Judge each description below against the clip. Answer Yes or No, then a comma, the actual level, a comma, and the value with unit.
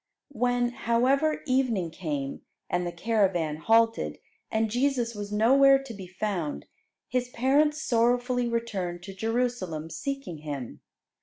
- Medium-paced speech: No, slow, 125 wpm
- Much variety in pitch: Yes, wide, 5.7 semitones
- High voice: Yes, high, 230 Hz